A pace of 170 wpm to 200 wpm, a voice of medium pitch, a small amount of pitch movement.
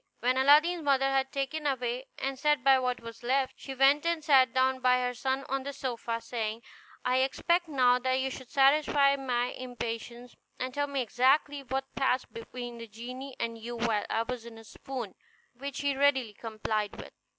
No: average, 190 wpm; very high, 260 Hz; narrow, 2.3 semitones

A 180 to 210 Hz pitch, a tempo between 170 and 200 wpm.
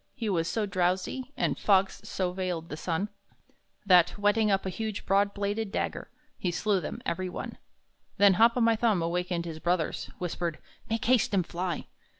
Yes: high, 190 Hz; average, 175 wpm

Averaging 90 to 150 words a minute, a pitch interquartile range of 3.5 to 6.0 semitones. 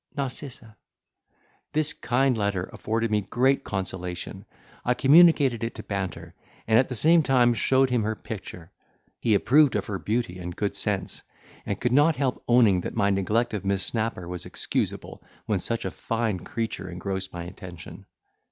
No: average, 165 wpm; average, 4.6 semitones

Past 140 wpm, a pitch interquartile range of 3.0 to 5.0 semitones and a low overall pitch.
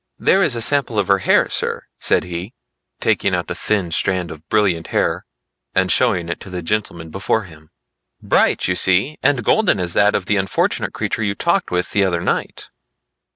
Yes: average, 195 wpm; average, 3.5 semitones; very low, 95 Hz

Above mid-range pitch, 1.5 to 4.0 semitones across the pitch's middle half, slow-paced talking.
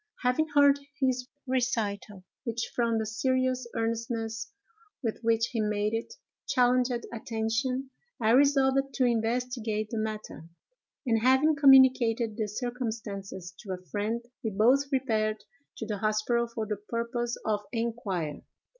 Yes: high, 230 Hz; average, 2.7 semitones; slow, 130 wpm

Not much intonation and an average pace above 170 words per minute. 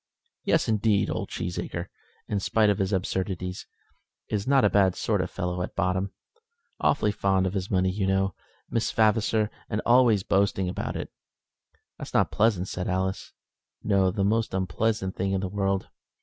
No: narrow, 2.2 semitones; average, 165 wpm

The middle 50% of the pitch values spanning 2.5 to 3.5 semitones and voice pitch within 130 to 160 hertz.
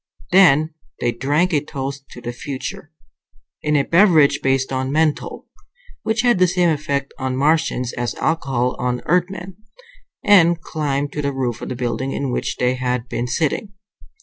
No: average, 4.1 semitones; medium, 140 Hz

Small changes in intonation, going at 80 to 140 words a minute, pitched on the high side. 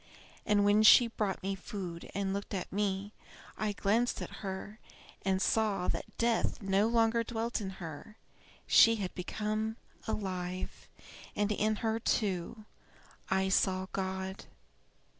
Yes: narrow, 2.3 semitones; slow, 135 wpm; high, 205 Hz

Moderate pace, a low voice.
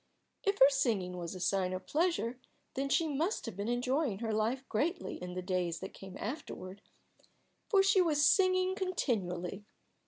No: average, 165 wpm; high, 240 Hz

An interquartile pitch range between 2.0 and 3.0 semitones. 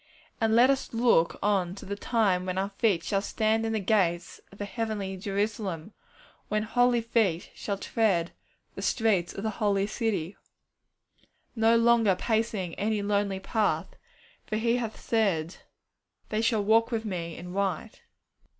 Yes: average, 2.7 semitones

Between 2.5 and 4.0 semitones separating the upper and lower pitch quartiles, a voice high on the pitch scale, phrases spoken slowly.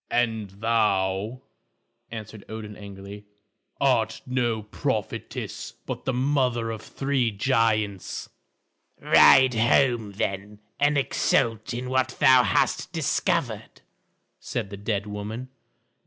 No: average, 3.5 semitones; low, 110 Hz; slow, 105 wpm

